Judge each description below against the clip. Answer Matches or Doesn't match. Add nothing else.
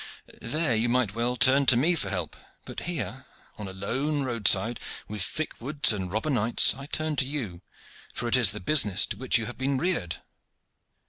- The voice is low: Matches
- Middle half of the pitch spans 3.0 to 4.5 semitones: Doesn't match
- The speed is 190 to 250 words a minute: Matches